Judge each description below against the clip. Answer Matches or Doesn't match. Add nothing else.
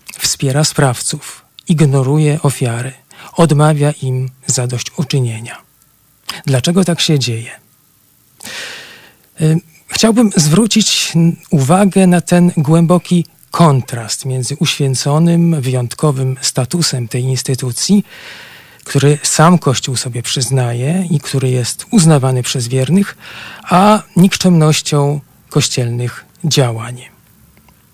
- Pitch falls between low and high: Matches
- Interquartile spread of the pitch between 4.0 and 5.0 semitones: Matches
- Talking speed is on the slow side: Matches